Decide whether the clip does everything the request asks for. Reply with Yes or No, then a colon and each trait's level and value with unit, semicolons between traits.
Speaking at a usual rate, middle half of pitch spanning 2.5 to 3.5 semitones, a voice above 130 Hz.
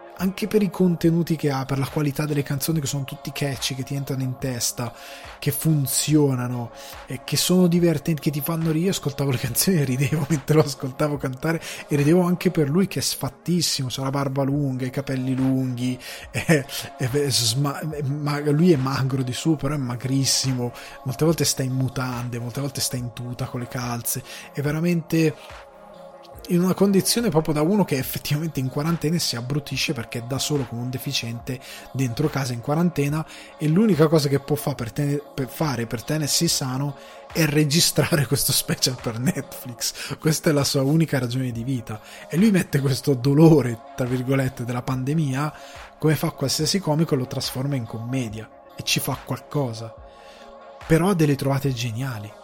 No: fast, 180 wpm; average, 2.9 semitones; medium, 140 Hz